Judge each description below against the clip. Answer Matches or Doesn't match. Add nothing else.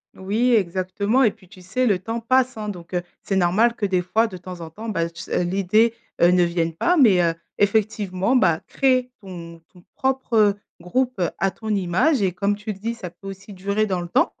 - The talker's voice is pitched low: Doesn't match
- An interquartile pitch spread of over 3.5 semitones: Matches